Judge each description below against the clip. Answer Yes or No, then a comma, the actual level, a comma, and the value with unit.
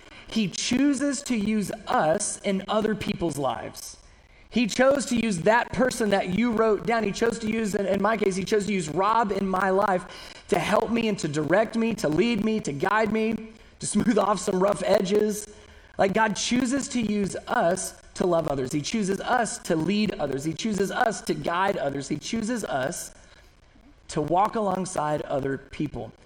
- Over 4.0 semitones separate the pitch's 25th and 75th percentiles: No, average, 3.3 semitones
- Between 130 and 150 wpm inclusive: No, average, 185 wpm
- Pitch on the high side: Yes, high, 210 Hz